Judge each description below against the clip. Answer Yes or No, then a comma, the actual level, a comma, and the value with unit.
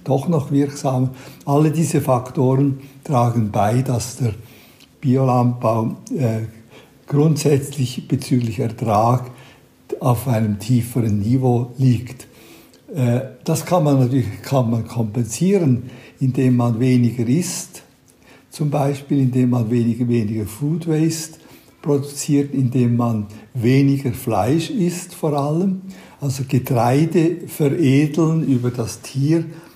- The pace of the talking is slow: Yes, slow, 110 wpm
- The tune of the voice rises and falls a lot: No, average, 3.1 semitones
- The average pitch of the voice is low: Yes, low, 130 Hz